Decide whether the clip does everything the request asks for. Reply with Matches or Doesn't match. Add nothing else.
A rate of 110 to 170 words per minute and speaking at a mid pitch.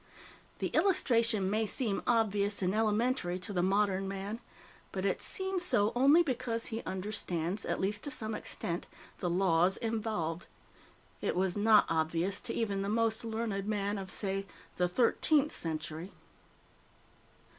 Doesn't match